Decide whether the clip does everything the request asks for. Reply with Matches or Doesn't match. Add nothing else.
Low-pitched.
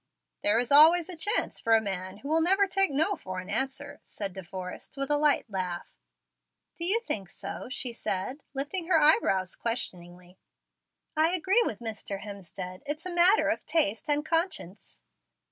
Doesn't match